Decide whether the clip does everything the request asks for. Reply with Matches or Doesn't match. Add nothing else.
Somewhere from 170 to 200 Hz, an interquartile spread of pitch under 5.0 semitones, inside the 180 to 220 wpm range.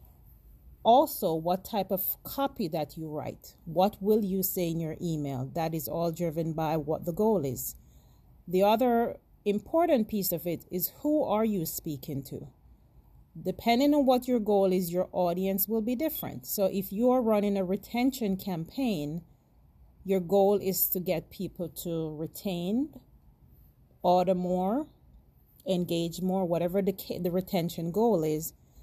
Doesn't match